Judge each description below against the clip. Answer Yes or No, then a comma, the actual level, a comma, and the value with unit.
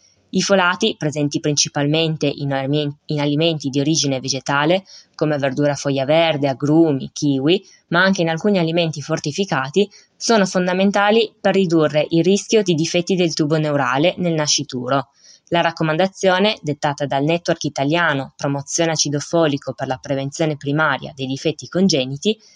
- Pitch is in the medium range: Yes, medium, 155 Hz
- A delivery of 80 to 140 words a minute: Yes, average, 130 wpm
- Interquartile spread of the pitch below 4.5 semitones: Yes, average, 3.7 semitones